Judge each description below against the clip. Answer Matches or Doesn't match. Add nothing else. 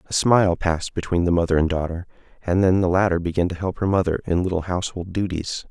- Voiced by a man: Matches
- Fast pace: Matches